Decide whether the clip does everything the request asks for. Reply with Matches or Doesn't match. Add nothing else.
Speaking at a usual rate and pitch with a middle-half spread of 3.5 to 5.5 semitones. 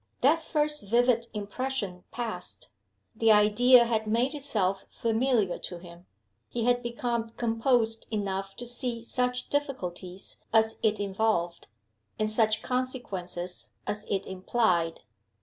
Doesn't match